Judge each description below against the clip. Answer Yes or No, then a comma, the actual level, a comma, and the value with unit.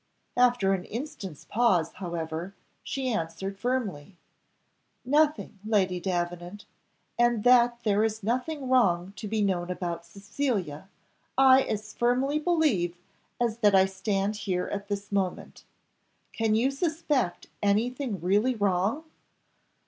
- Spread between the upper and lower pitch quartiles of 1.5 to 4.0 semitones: No, average, 4.9 semitones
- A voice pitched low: No, high, 205 Hz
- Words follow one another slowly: Yes, slow, 120 wpm